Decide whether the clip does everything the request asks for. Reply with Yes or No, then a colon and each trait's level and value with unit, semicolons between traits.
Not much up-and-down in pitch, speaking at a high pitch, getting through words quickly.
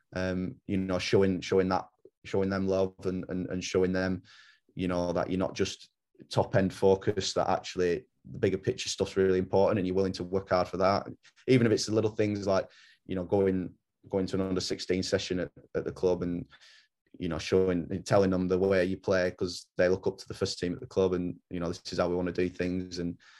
No: narrow, 1.0 semitones; very low, 95 Hz; fast, 240 wpm